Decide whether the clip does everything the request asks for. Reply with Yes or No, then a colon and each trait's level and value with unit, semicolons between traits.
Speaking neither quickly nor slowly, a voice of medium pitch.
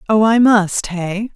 No: average, 175 wpm; high, 205 Hz